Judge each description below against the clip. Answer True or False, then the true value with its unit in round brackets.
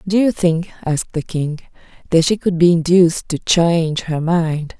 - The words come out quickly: False (190 wpm)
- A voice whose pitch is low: False (170 Hz)